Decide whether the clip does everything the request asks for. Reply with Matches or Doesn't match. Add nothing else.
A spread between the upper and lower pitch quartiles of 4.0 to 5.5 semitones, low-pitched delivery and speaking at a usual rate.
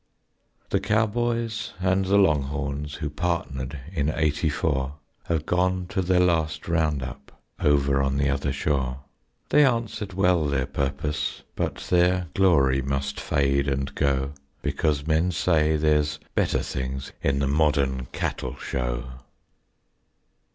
Doesn't match